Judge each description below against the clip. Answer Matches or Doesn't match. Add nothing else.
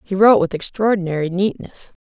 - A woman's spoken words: Matches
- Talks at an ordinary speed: Matches